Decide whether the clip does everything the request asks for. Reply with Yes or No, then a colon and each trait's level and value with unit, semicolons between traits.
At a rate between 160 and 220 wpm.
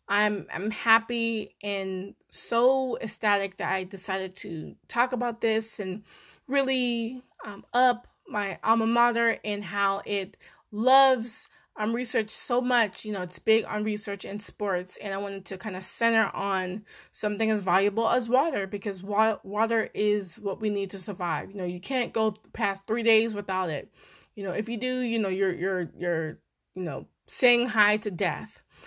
Yes: average, 175 wpm